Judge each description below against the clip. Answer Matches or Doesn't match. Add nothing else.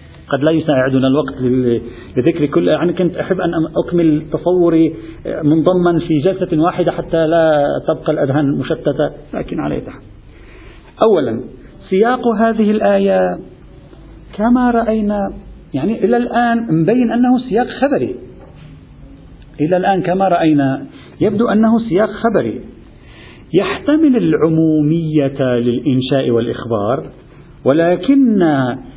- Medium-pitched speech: Matches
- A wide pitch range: Matches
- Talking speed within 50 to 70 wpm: Doesn't match